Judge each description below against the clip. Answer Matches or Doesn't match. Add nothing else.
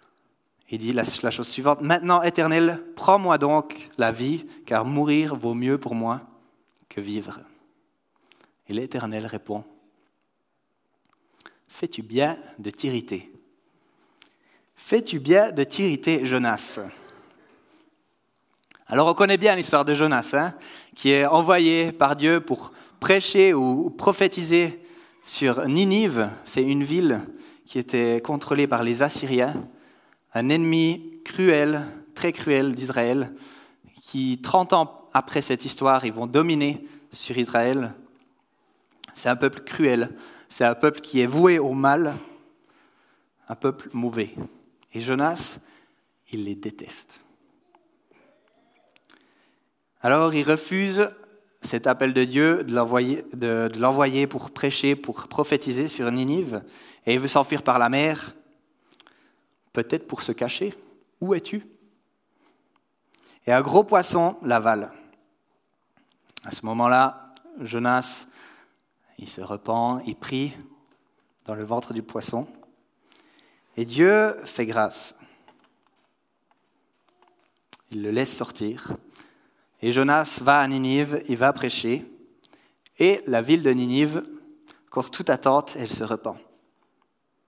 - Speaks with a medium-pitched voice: Matches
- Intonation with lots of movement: Matches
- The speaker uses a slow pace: Matches